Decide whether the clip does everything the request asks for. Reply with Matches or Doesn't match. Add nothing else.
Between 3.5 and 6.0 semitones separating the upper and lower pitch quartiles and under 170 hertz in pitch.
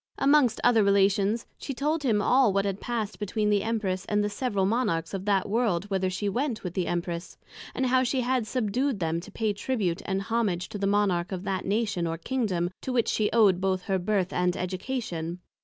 Doesn't match